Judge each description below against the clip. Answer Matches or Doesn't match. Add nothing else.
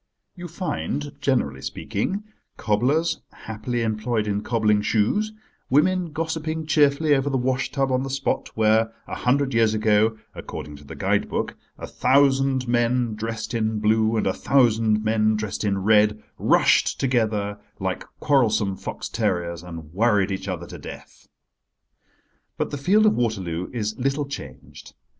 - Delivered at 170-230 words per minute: Doesn't match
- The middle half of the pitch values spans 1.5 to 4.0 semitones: Doesn't match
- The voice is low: Matches